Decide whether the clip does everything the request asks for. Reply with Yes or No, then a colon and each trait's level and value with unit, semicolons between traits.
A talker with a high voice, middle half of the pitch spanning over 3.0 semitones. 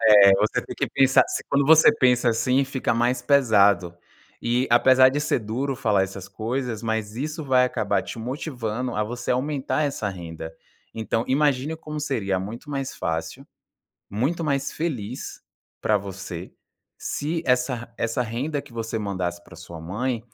No: low, 120 Hz; average, 4.6 semitones